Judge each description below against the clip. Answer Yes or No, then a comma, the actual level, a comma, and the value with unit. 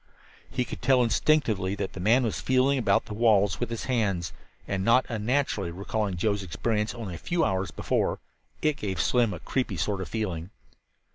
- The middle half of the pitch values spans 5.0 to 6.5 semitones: No, average, 4.3 semitones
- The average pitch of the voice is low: Yes, low, 110 Hz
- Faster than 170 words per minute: Yes, average, 185 wpm